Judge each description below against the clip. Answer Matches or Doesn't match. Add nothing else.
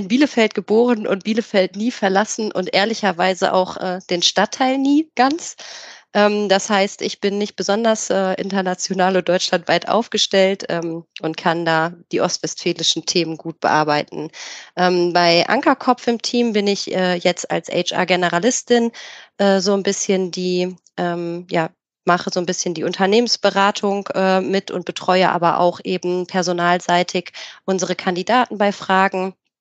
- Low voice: Doesn't match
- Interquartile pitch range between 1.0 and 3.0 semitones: Matches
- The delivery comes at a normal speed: Matches